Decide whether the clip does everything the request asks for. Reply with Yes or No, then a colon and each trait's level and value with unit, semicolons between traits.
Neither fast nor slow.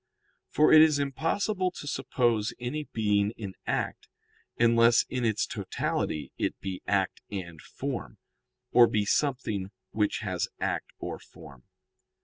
No: slow, 130 wpm